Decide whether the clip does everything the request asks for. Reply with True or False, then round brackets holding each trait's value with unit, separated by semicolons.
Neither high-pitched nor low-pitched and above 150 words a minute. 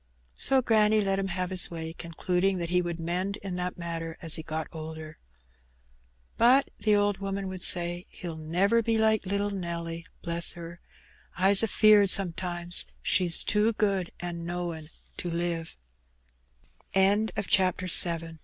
False (180 Hz; 135 wpm)